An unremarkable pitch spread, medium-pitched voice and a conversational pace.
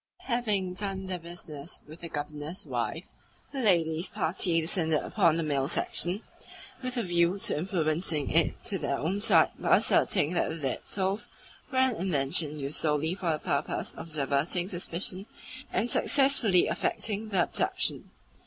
Yes: average, 4.0 semitones; medium, 175 Hz; average, 155 wpm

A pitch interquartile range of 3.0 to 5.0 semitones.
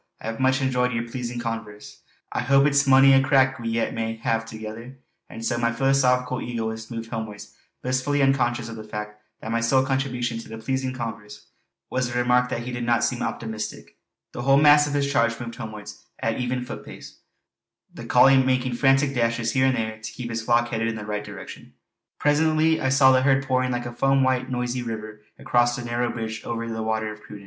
No: narrow, 2.6 semitones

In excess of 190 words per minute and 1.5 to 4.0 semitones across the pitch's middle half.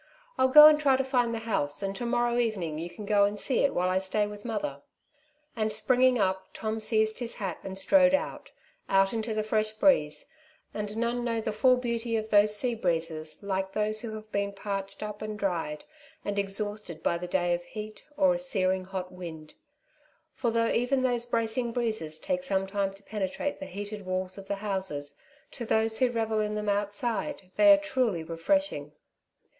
Yes: average, 200 wpm; average, 3.7 semitones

